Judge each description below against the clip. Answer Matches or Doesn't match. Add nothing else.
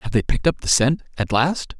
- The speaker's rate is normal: Doesn't match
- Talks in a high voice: Doesn't match